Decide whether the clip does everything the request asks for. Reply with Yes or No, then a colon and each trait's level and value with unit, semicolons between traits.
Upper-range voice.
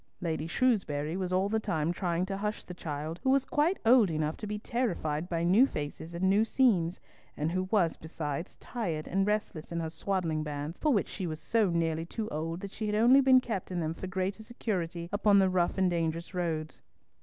No: medium, 180 Hz